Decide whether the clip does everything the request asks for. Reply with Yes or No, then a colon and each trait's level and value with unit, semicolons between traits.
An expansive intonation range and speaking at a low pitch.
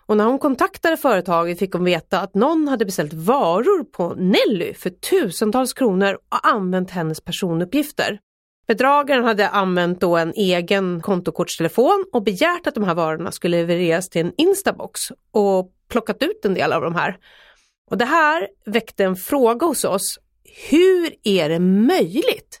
No: wide, 7.7 semitones; high, 210 Hz